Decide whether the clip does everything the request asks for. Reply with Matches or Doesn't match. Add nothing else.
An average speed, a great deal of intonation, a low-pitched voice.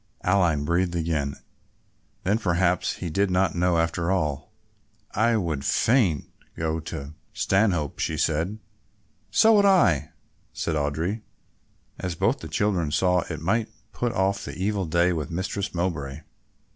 Doesn't match